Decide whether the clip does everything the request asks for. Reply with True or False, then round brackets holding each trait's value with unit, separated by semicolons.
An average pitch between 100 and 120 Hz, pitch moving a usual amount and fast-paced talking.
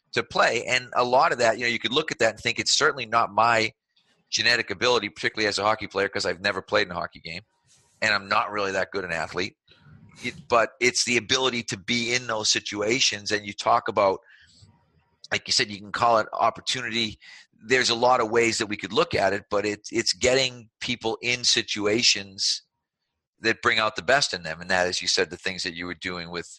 True (110 Hz; 3.5 semitones; 230 wpm)